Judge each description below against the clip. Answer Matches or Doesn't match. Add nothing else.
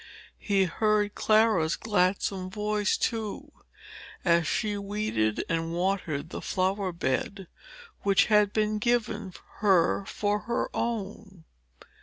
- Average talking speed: Doesn't match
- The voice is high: Matches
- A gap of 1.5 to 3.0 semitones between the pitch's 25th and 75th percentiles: Matches